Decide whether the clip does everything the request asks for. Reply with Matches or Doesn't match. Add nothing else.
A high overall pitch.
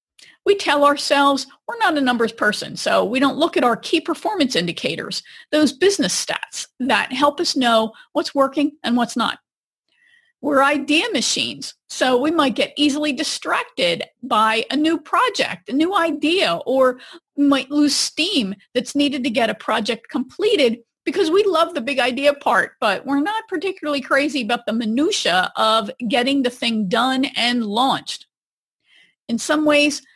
Matches